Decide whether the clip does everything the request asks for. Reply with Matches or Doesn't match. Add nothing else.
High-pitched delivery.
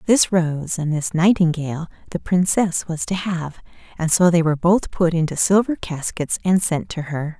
Doesn't match